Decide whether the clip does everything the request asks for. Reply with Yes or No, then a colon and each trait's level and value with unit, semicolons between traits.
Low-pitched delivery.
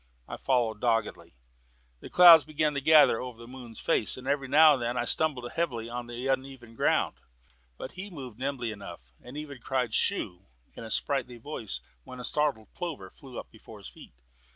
Yes: low, 125 Hz